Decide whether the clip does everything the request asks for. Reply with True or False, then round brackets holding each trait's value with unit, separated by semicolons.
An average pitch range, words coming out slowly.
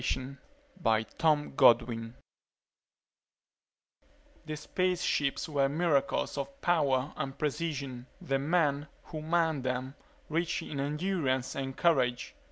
True (3.7 semitones; 95 wpm)